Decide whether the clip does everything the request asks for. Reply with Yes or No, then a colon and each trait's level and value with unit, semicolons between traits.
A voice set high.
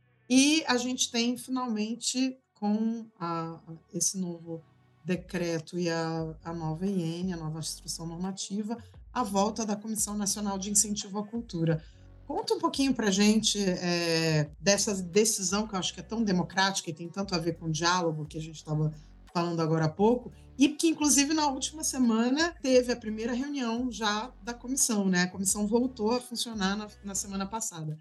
Yes: high, 200 Hz